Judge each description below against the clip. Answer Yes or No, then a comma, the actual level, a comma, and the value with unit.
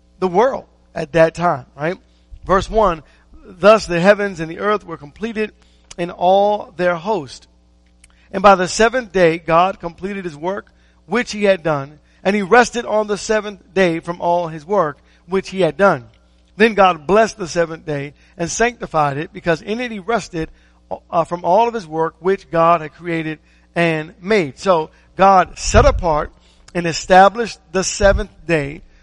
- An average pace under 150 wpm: No, average, 170 wpm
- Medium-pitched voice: Yes, medium, 175 Hz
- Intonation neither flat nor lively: Yes, average, 3.9 semitones